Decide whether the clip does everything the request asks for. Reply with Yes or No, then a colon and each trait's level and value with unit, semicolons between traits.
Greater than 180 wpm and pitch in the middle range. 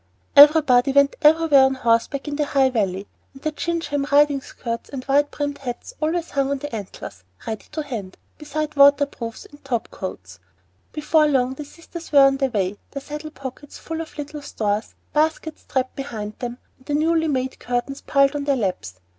No: average, 190 wpm; very high, 275 Hz